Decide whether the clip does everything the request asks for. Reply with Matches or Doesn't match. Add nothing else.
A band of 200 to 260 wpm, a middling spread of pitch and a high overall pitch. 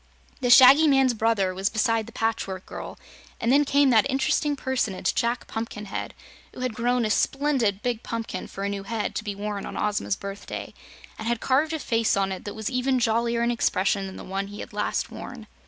Matches